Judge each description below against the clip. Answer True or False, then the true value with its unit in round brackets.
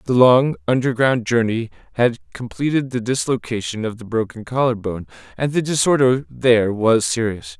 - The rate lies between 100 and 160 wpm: True (150 wpm)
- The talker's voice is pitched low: True (120 Hz)